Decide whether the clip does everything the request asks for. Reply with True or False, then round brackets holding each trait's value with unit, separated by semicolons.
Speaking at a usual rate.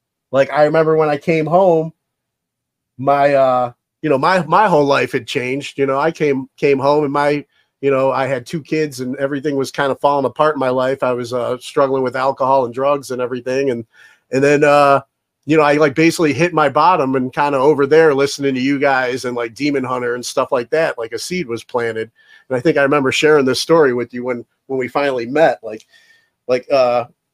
False (225 wpm)